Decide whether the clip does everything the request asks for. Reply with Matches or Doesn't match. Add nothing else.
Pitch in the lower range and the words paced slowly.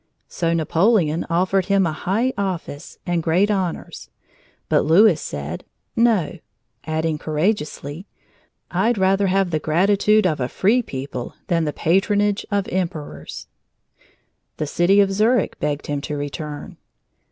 Doesn't match